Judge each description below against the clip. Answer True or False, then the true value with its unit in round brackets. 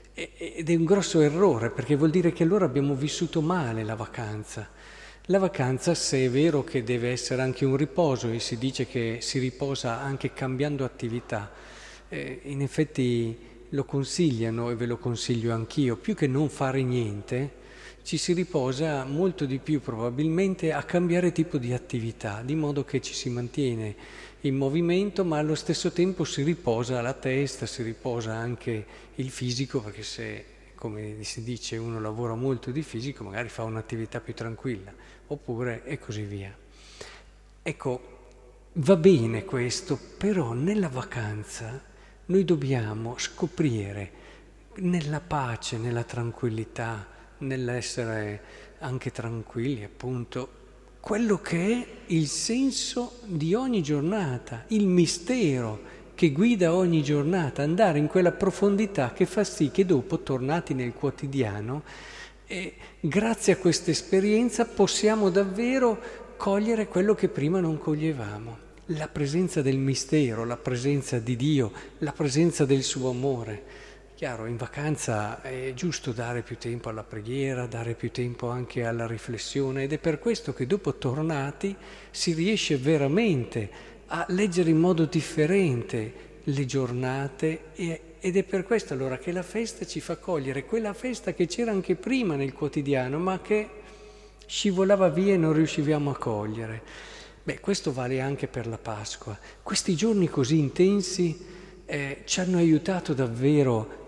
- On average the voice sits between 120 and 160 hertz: True (140 Hz)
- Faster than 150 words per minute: False (145 wpm)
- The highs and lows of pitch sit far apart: True (6.3 semitones)